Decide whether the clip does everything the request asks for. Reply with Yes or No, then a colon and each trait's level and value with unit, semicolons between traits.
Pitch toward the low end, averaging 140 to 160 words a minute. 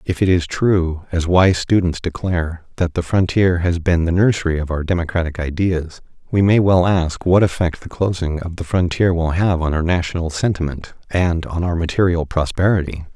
No: very low, 85 Hz; average, 185 wpm